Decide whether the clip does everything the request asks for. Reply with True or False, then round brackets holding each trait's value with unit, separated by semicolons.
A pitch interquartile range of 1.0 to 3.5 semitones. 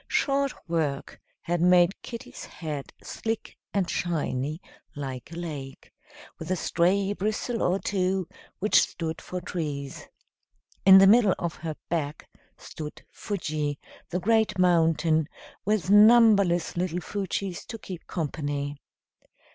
False (4.1 semitones)